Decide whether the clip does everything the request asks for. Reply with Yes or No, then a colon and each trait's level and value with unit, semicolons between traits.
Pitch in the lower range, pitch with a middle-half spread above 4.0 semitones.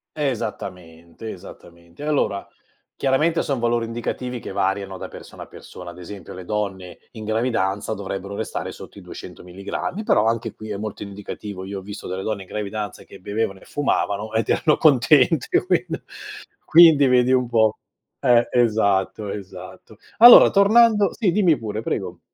Yes: low, 110 Hz; average, 4.6 semitones